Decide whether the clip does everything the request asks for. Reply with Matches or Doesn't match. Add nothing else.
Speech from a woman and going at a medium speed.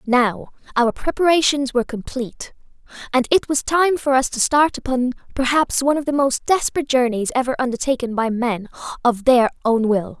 Matches